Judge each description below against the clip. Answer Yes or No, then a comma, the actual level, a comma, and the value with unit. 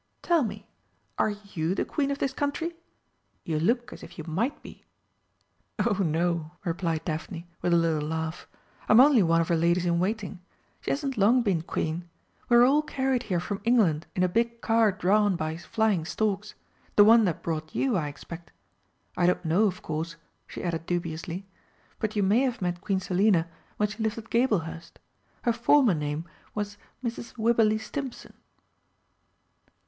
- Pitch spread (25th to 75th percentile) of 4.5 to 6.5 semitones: Yes, wide, 5.5 semitones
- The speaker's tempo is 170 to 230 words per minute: Yes, average, 175 wpm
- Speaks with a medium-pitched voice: No, high, 195 Hz